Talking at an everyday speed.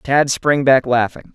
Yes: average, 180 wpm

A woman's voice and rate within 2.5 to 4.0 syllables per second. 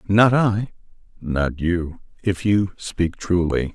No: male; 3.2 syllables/s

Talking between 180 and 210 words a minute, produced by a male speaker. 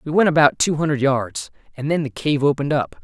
No: fast, 235 wpm; male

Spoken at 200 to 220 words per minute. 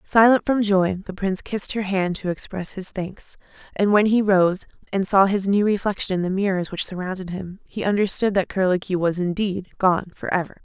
Yes: fast, 205 wpm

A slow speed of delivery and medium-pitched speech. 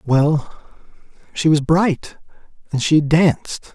Yes: slow, 110 wpm; medium, 155 Hz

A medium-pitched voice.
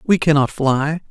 Yes: medium, 150 Hz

